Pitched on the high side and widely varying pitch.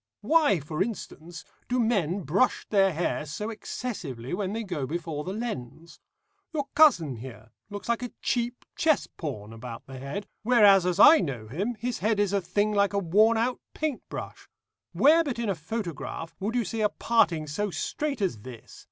Yes: high, 200 Hz; wide, 7.0 semitones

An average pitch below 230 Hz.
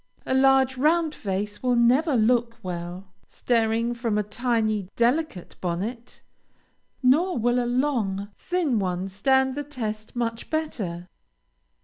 No: high, 235 Hz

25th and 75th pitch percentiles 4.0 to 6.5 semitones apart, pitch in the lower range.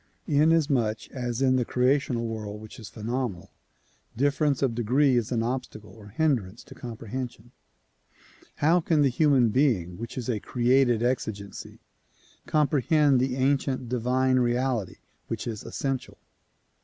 No: average, 3.1 semitones; low, 125 Hz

